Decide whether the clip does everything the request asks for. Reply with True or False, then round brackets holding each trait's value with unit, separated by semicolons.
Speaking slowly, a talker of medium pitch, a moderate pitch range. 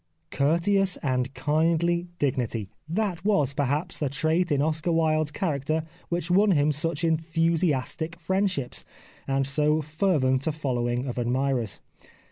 True (125 wpm; 155 Hz; 3.6 semitones)